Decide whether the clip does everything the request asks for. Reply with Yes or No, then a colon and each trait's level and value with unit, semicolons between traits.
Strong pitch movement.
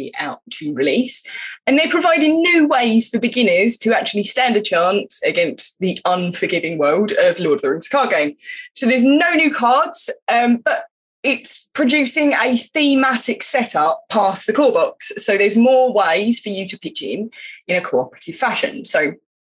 Yes: wide, 6.4 semitones